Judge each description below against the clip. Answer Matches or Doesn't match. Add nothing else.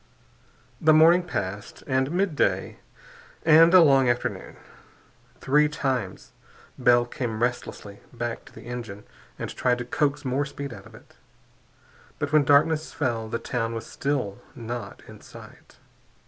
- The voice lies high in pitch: Doesn't match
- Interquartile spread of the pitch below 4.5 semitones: Matches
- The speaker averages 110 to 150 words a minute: Matches